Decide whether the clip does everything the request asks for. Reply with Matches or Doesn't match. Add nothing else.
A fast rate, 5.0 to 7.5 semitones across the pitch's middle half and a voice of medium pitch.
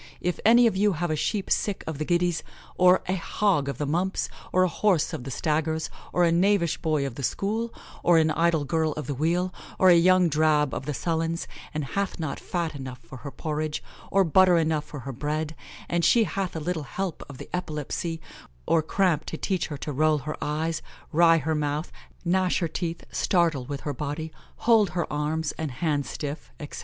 Doesn't match